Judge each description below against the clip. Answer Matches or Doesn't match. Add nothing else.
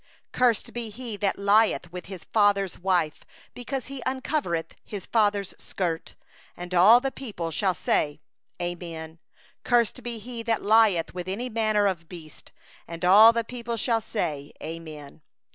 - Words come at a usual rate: Matches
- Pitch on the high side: Matches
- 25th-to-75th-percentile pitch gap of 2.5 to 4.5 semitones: Doesn't match